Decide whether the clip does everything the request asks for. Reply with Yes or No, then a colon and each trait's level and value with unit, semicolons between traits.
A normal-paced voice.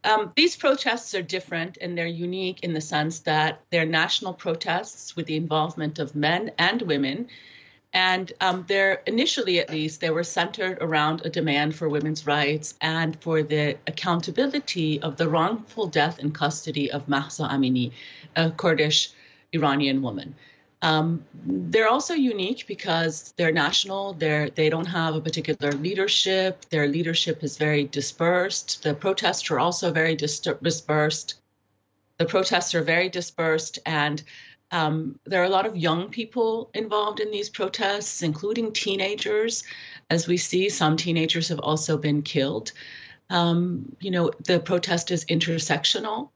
Yes: average, 150 wpm